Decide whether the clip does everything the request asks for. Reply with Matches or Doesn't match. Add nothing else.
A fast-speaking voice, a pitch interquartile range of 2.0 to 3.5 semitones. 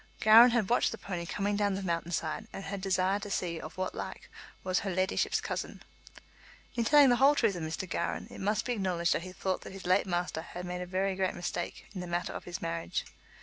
Matches